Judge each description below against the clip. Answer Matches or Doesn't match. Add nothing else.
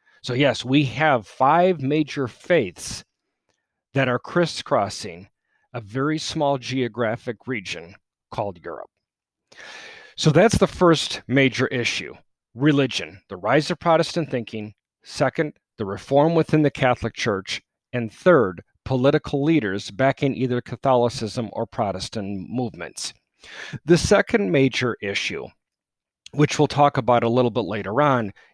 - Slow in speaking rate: Matches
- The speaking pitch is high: Doesn't match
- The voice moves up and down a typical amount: Matches